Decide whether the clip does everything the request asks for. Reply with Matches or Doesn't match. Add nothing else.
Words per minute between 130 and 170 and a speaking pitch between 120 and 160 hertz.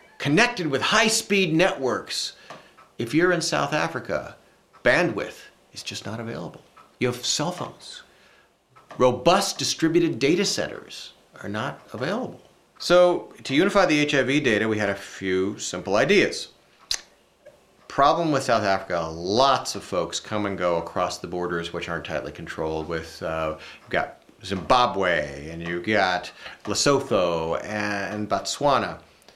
Doesn't match